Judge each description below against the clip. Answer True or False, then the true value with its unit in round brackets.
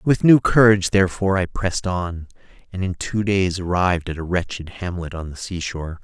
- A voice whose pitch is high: False (90 Hz)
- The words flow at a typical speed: True (190 wpm)